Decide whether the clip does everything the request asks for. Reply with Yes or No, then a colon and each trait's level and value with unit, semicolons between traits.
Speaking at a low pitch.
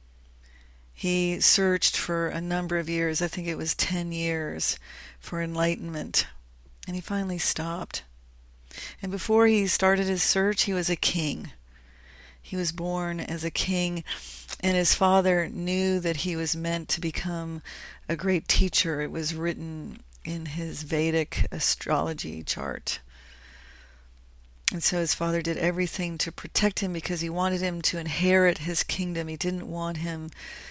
No: medium, 170 Hz